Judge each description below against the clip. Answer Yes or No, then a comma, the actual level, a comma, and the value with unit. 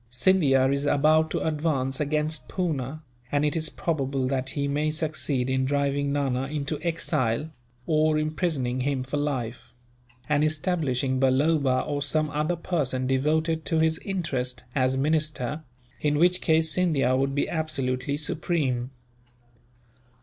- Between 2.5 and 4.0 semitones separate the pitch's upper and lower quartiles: Yes, average, 3.0 semitones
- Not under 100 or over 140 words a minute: Yes, slow, 135 wpm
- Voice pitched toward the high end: No, medium, 145 Hz